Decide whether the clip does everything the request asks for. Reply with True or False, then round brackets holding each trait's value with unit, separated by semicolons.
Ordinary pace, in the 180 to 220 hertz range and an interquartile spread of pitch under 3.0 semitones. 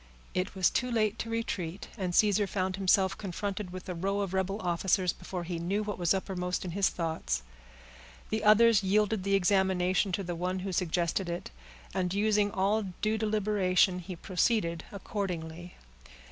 True (165 wpm; 190 Hz; 2.4 semitones)